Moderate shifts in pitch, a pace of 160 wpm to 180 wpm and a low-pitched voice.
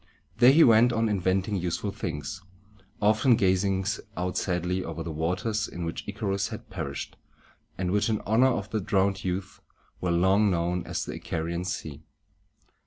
Yes: average, 3.3 semitones; average, 170 wpm; very low, 95 Hz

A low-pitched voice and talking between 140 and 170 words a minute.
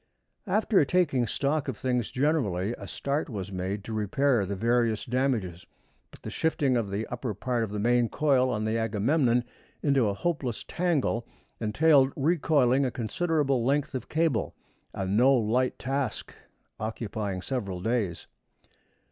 Yes: low, 125 Hz; average, 150 wpm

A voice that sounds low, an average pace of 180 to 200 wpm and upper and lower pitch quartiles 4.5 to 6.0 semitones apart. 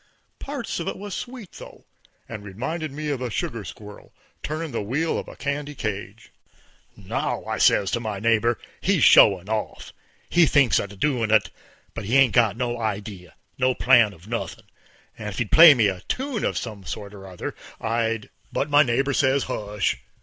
Yes: low, 115 Hz; average, 190 wpm; wide, 5.4 semitones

